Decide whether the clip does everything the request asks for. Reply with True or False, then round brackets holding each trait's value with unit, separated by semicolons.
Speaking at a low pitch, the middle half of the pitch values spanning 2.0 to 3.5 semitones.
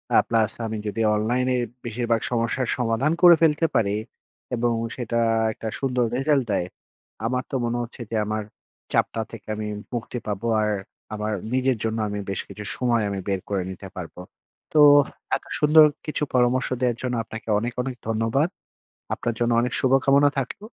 True (120 Hz; 2.9 semitones)